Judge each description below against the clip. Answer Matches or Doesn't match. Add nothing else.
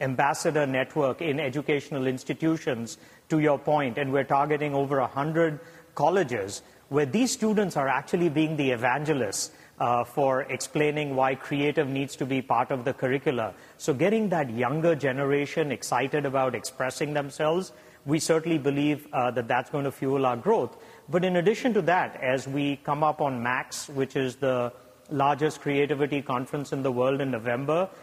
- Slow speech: Doesn't match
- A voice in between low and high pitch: Matches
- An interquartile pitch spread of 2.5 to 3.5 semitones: Matches